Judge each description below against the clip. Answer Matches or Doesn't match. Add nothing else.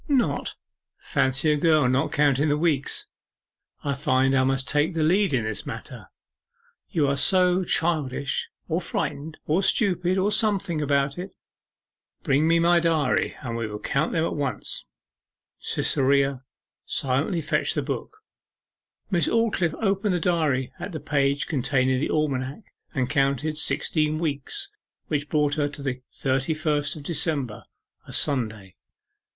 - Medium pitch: Matches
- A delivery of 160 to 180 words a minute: Doesn't match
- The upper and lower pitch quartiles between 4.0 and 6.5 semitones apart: Doesn't match